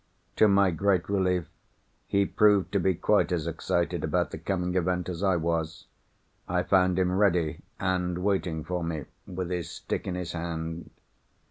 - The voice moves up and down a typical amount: No, narrow, 2.0 semitones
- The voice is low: Yes, very low, 90 Hz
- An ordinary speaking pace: Yes, average, 165 wpm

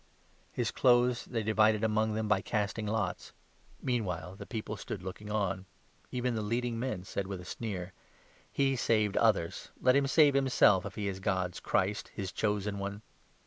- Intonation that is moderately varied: Yes, average, 3.1 semitones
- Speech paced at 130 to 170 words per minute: No, average, 185 wpm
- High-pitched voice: No, low, 105 Hz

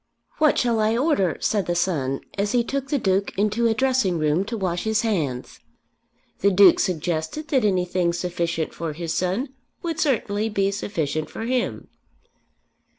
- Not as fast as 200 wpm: Yes, average, 160 wpm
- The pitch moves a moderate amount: Yes, average, 5.0 semitones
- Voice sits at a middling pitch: No, high, 200 Hz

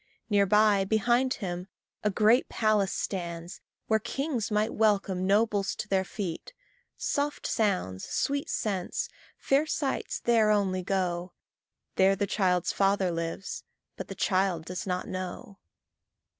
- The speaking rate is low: Yes, slow, 130 wpm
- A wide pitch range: No, average, 2.9 semitones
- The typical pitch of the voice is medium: No, high, 195 Hz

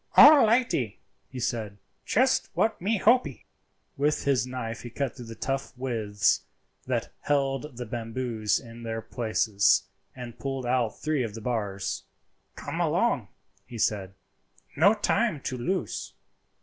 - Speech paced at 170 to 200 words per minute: No, slow, 135 wpm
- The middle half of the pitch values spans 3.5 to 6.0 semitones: Yes, average, 4.1 semitones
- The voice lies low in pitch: Yes, low, 125 Hz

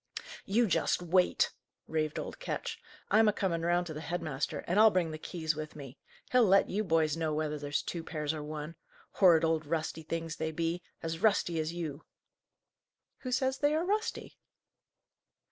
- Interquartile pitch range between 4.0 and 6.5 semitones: No, average, 3.6 semitones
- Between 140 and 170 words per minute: No, average, 180 wpm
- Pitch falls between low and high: Yes, medium, 165 Hz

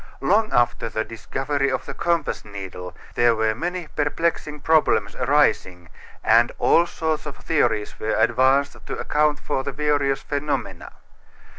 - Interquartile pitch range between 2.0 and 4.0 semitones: No, average, 4.9 semitones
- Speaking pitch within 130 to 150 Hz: Yes, medium, 140 Hz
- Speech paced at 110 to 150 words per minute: Yes, average, 140 wpm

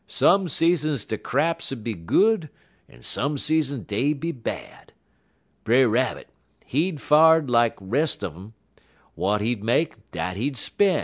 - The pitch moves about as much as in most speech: No, wide, 6.3 semitones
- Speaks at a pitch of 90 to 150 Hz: Yes, low, 135 Hz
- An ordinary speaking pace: Yes, average, 150 wpm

